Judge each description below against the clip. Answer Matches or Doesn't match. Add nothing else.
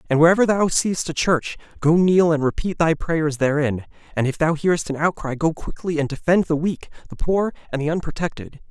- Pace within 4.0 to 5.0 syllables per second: Doesn't match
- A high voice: Doesn't match